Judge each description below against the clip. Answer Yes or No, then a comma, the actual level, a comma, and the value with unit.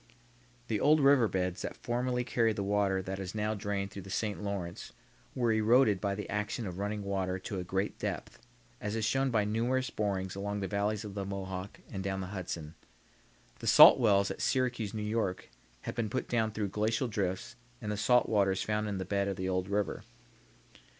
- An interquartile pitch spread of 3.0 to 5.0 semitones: No, narrow, 2.4 semitones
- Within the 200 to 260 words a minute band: Yes, fast, 205 wpm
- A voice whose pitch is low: Yes, low, 105 Hz